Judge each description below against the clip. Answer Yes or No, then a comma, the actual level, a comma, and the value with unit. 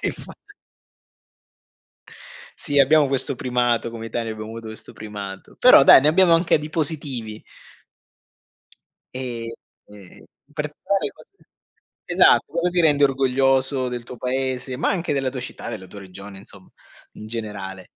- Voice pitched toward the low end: Yes, low, 125 Hz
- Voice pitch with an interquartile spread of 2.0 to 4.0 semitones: No, average, 4.6 semitones